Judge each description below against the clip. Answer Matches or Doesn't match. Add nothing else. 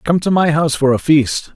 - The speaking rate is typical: Doesn't match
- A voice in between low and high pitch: Matches